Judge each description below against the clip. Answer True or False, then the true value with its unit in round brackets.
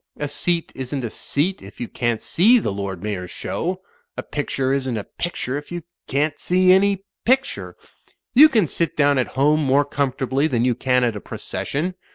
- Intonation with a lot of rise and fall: True (5.7 semitones)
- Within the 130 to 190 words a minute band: False (200 wpm)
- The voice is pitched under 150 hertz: True (140 Hz)